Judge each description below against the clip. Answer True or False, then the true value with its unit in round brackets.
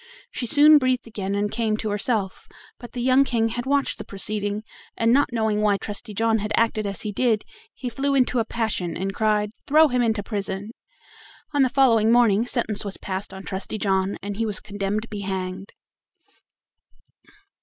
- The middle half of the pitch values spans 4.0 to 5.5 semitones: False (3.1 semitones)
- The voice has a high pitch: True (215 Hz)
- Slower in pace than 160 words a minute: False (185 wpm)